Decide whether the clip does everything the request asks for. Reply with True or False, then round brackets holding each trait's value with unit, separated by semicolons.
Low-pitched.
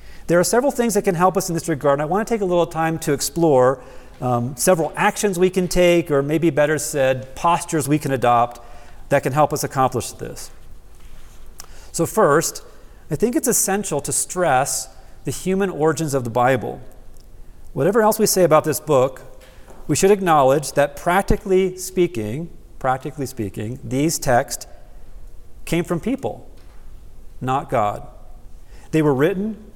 False (150 Hz)